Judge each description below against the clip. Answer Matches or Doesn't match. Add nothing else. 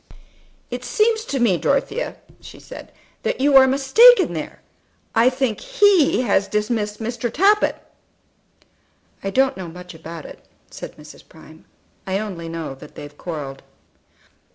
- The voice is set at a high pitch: Matches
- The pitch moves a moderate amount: Doesn't match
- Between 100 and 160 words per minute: Matches